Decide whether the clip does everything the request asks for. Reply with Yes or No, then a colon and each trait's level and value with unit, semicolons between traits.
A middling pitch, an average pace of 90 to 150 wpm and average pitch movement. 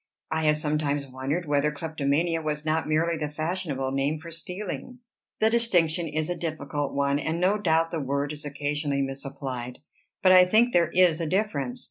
No: medium, 155 Hz; average, 175 wpm; average, 3.1 semitones